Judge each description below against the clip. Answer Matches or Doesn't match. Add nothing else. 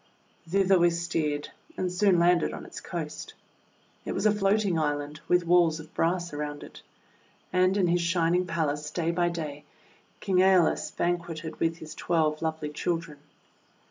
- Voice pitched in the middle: Matches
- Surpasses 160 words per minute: Doesn't match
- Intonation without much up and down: Matches